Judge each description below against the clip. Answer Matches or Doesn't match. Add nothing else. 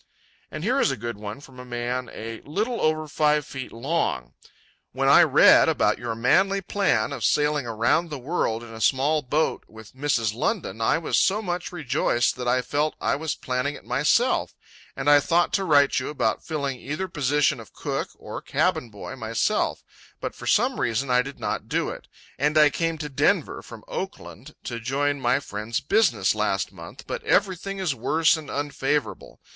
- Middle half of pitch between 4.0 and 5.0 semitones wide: Matches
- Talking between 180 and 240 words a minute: Matches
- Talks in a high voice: Doesn't match